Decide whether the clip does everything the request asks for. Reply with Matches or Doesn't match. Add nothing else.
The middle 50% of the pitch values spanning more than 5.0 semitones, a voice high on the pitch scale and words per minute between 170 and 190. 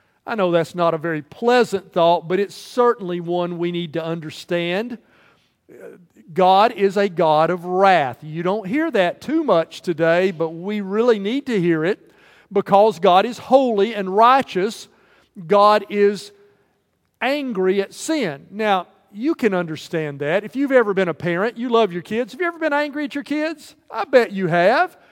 Matches